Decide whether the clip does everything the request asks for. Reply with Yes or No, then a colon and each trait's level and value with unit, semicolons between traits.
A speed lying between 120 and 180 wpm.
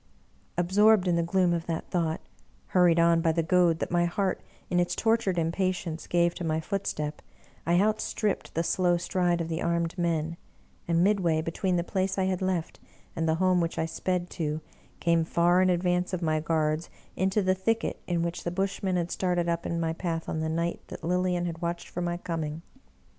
No: fast, 205 wpm